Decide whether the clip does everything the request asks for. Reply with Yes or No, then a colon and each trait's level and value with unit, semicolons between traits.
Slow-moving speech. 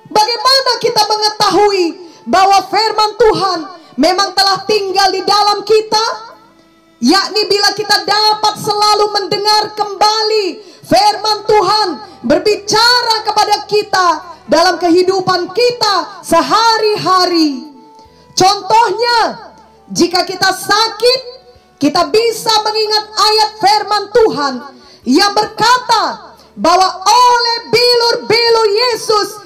Yes: slow, 90 wpm